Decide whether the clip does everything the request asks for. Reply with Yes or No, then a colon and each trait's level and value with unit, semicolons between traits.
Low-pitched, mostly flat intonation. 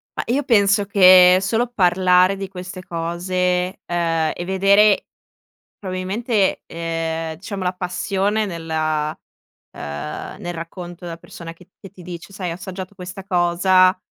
No: medium, 180 Hz; narrow, 2.2 semitones